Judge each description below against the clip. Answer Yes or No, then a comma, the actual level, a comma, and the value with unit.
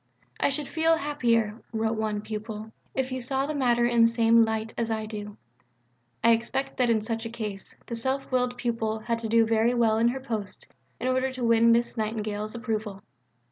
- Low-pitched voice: No, high, 230 Hz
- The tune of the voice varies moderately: No, narrow, 2.1 semitones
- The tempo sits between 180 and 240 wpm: Yes, average, 200 wpm